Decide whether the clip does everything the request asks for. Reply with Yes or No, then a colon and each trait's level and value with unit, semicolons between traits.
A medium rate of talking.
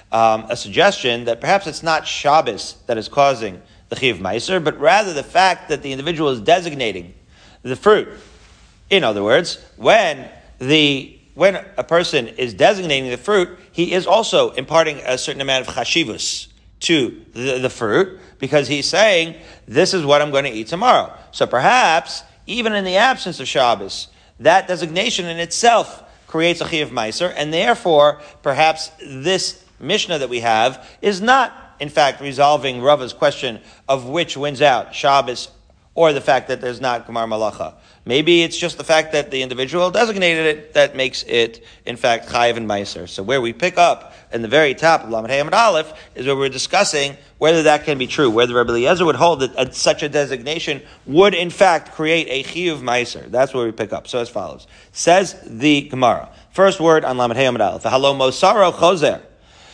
Yes: average, 180 wpm